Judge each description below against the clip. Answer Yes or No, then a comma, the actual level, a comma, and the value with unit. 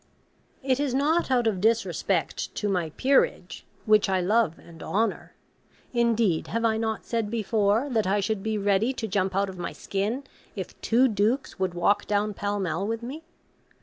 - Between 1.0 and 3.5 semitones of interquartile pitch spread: Yes, average, 3.1 semitones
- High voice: Yes, high, 215 Hz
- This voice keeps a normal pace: Yes, average, 180 wpm